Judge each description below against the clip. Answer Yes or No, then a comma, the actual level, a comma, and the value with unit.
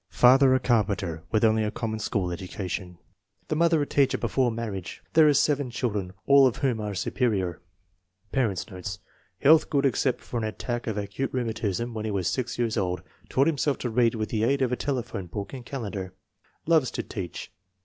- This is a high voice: No, low, 115 Hz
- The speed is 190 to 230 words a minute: Yes, average, 195 wpm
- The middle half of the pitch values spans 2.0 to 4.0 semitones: No, average, 4.8 semitones